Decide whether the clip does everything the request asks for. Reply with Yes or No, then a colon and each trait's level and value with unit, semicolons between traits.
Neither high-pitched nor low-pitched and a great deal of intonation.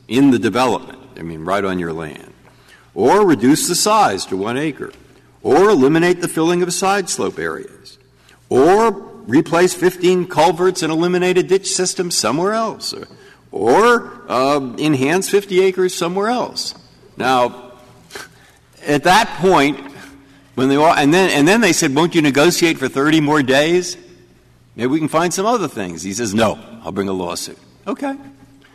Yes: medium, 160 Hz; wide, 6.0 semitones